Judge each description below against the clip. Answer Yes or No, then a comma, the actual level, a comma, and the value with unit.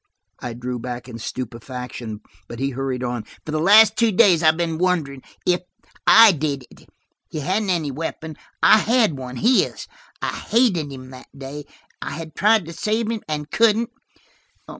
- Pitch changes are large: Yes, wide, 7.6 semitones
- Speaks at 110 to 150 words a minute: No, average, 165 wpm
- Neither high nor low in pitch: Yes, medium, 155 Hz